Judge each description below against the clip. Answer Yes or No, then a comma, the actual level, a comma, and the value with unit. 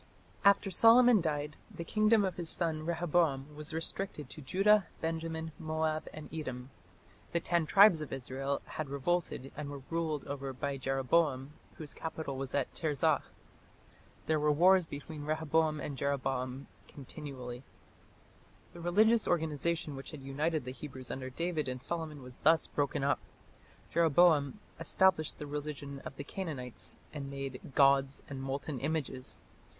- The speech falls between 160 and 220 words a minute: No, average, 145 wpm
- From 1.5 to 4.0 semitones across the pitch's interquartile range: Yes, average, 3.3 semitones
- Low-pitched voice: No, medium, 150 Hz